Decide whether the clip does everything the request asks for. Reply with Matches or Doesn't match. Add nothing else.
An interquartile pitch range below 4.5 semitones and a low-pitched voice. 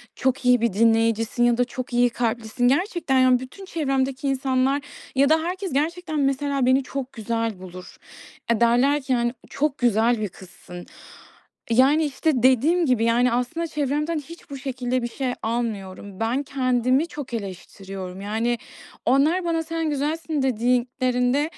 Doesn't match